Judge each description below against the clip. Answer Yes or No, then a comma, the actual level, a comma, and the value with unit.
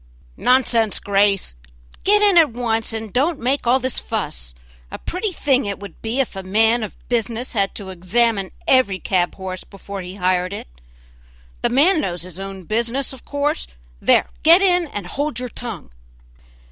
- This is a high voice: Yes, high, 225 Hz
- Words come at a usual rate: Yes, average, 170 wpm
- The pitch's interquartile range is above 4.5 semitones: Yes, wide, 5.4 semitones